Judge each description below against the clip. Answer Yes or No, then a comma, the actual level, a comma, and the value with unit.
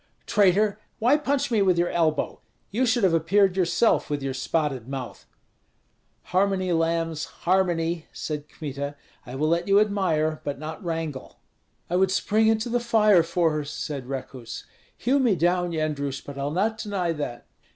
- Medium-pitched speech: Yes, medium, 170 Hz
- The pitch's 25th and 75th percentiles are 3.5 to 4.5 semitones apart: No, average, 5.0 semitones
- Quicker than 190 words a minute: No, average, 160 wpm